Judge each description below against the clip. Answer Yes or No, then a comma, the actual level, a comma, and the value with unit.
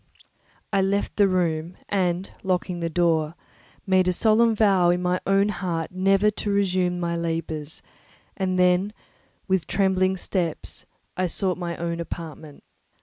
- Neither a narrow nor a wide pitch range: No, narrow, 2.3 semitones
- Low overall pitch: No, medium, 180 Hz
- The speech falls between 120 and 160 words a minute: Yes, average, 145 wpm